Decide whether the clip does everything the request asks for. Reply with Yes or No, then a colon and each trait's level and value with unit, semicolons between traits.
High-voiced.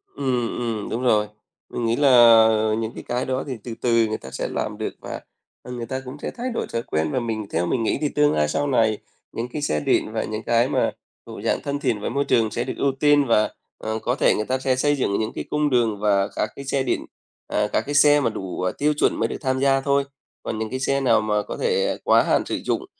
No: low, 120 Hz